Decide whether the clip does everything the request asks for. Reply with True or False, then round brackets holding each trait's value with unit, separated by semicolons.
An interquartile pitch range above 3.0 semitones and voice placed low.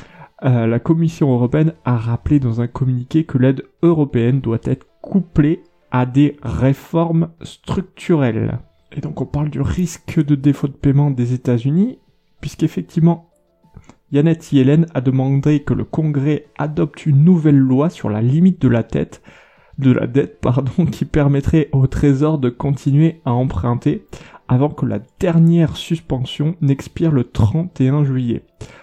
False (3.9 semitones; 145 Hz)